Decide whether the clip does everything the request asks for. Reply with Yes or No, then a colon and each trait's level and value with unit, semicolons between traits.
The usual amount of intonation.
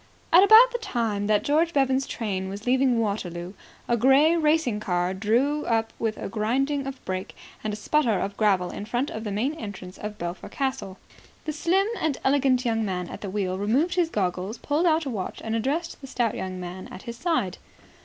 No: wide, 6.2 semitones